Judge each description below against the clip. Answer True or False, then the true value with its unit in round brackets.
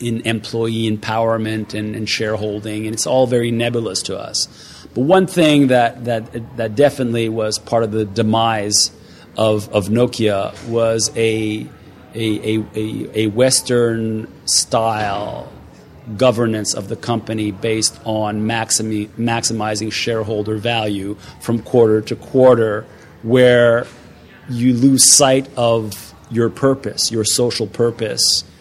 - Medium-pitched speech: False (115 Hz)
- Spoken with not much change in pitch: True (1.7 semitones)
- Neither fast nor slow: False (125 wpm)